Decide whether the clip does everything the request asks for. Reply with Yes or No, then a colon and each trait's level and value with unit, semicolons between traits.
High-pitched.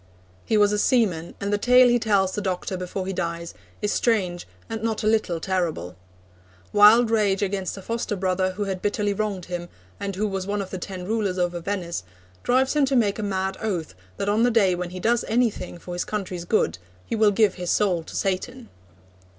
Yes: high, 200 Hz